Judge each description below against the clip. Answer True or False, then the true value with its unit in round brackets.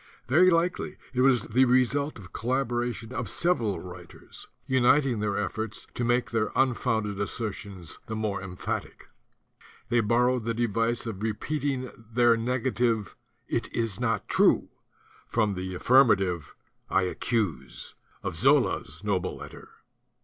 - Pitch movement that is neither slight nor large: True (3.5 semitones)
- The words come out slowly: True (130 wpm)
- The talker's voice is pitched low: True (115 Hz)